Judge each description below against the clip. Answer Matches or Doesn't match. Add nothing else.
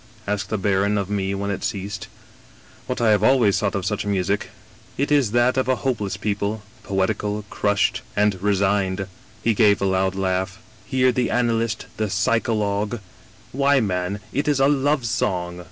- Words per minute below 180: Doesn't match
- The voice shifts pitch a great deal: Doesn't match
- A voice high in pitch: Doesn't match